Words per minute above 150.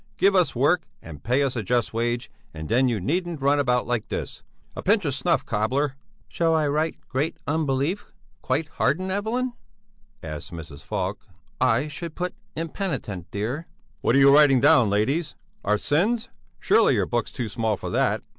Yes: average, 175 wpm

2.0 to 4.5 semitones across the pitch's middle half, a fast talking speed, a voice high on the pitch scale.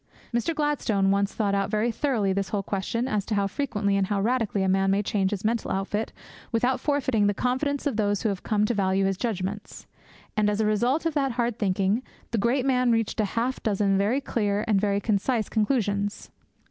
Yes: average, 3.3 semitones; fast, 210 wpm; high, 210 Hz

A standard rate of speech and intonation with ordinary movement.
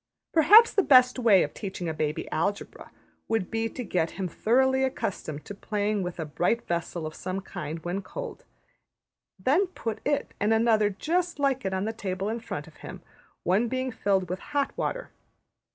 No: average, 185 wpm; wide, 6.0 semitones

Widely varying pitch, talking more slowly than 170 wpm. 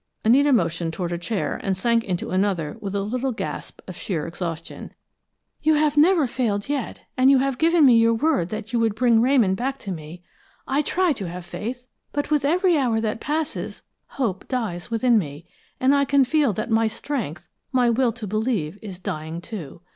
No: wide, 6.4 semitones; average, 195 wpm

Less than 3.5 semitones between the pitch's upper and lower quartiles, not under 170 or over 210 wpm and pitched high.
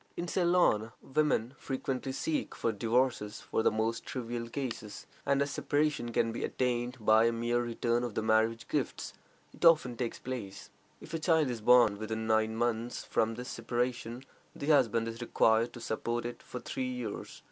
No: narrow, 2.4 semitones; average, 175 wpm; low, 120 Hz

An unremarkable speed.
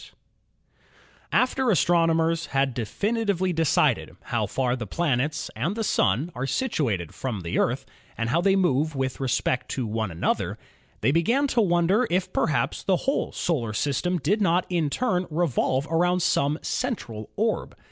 Yes: average, 165 wpm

